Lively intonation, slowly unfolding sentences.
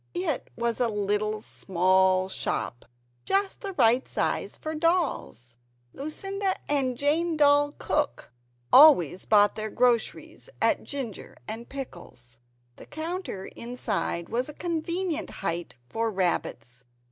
Yes: wide, 8.5 semitones; slow, 120 wpm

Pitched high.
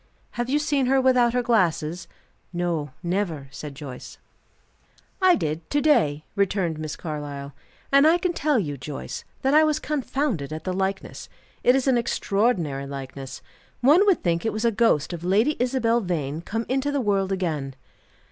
Yes: high, 195 Hz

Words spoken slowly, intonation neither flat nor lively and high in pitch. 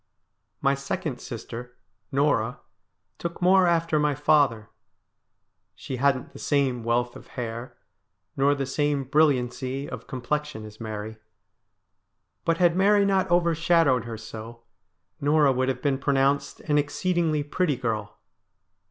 No: slow, 125 wpm; average, 3.9 semitones; medium, 140 Hz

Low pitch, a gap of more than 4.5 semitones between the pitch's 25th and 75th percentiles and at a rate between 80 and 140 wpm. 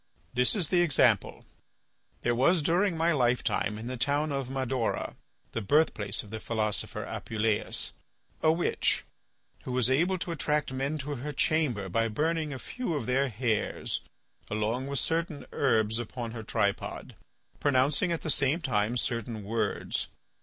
No: low, 130 Hz; average, 5.2 semitones; average, 155 wpm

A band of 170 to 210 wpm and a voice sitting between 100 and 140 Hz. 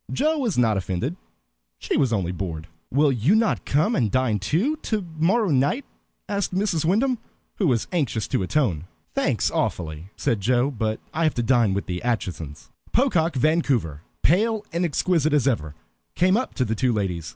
Yes: average, 175 wpm; low, 135 Hz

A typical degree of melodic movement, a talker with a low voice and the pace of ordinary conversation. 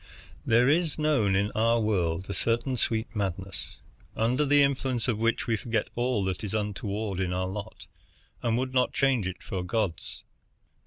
Yes: average, 4.2 semitones; low, 110 Hz; average, 175 wpm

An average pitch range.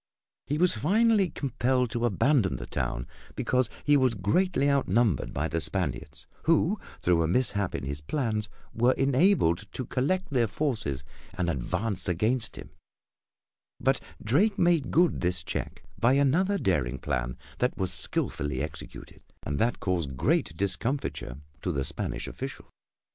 No: wide, 8.8 semitones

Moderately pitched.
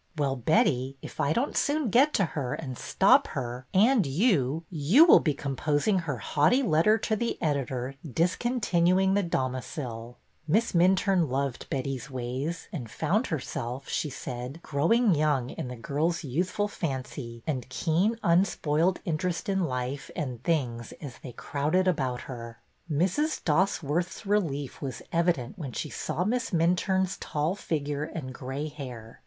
Yes: medium, 150 Hz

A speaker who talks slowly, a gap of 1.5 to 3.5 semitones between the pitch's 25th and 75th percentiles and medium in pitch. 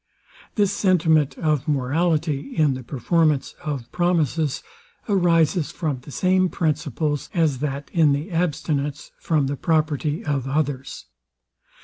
Yes: slow, 120 wpm; average, 3.1 semitones; medium, 155 Hz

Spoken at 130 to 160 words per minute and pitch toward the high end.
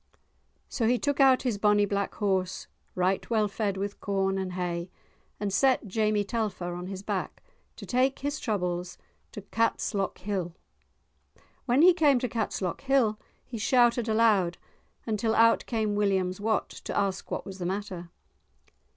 Yes: average, 150 wpm; high, 205 Hz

